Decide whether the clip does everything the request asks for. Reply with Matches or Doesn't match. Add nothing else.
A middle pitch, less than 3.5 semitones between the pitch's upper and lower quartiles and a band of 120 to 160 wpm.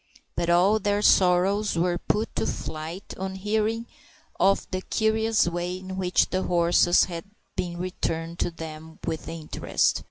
Matches